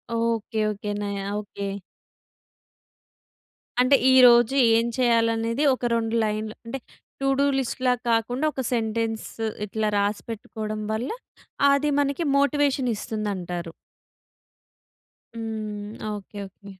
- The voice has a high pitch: Yes, high, 225 Hz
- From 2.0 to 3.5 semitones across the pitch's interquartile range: Yes, average, 2.9 semitones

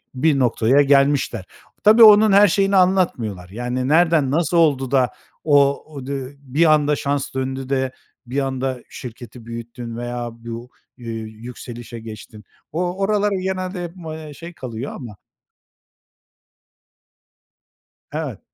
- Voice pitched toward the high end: No, low, 135 Hz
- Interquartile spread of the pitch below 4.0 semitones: No, wide, 5.5 semitones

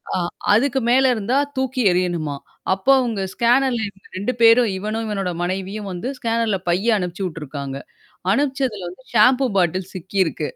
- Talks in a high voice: Yes, high, 205 Hz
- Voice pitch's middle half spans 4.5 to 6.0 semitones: Yes, average, 4.9 semitones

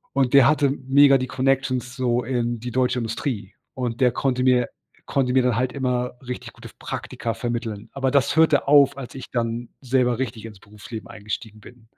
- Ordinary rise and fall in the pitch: No, narrow, 2.3 semitones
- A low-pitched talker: Yes, low, 125 Hz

